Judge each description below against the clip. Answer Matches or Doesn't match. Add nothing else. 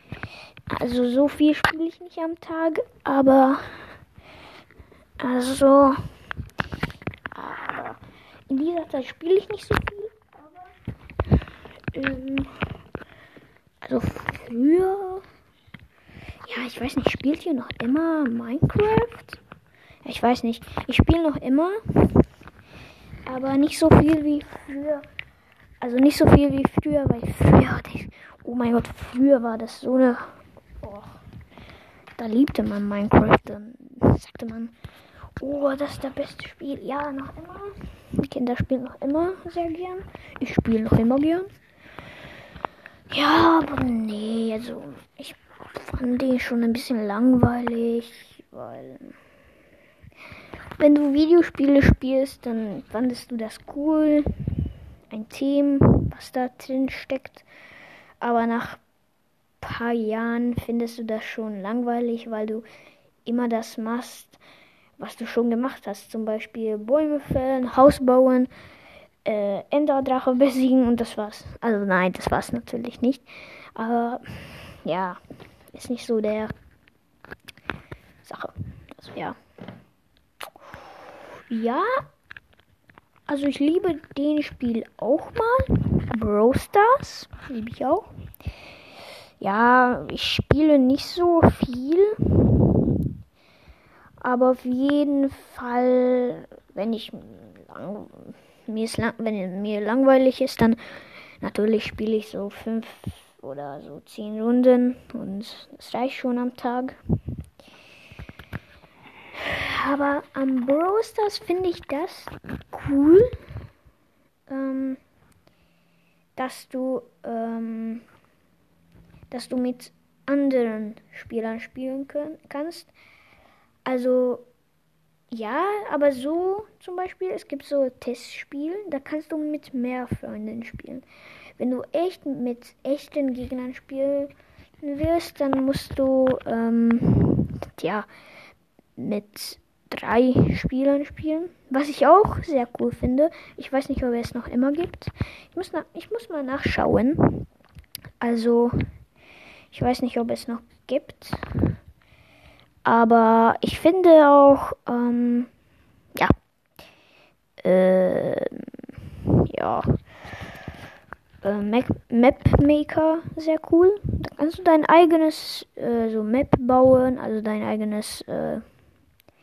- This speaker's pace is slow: Matches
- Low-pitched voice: Doesn't match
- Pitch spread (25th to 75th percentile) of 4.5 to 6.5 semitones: Doesn't match